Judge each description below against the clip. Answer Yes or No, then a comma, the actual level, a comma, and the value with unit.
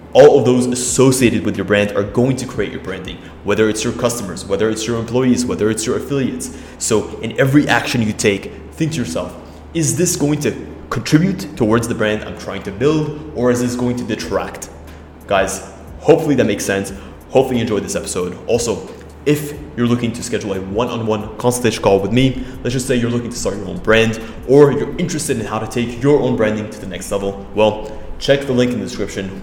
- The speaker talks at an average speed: No, fast, 220 wpm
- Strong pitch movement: No, average, 4.2 semitones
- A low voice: Yes, low, 115 Hz